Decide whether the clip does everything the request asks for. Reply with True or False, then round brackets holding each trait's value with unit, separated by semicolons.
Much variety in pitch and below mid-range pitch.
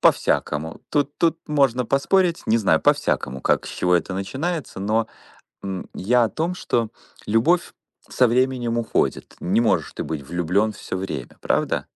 True (6.5 semitones; 115 Hz)